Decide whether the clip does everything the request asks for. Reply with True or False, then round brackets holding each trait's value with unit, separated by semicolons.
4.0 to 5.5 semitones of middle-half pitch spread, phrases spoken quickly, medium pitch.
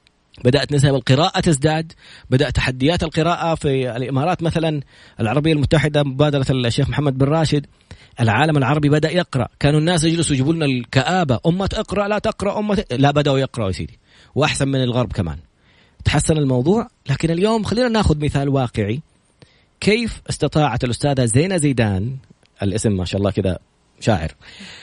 True (4.6 semitones; 145 wpm; 145 Hz)